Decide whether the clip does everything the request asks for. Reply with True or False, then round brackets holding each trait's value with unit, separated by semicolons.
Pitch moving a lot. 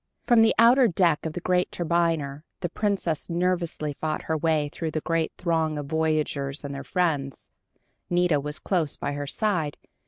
False (3.1 semitones)